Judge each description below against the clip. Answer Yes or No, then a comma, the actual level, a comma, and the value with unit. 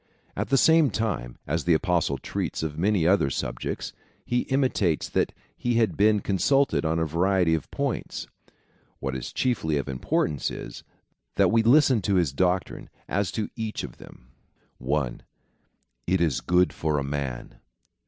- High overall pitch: No, very low, 90 Hz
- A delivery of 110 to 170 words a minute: Yes, average, 160 wpm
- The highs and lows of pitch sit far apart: Yes, wide, 6.5 semitones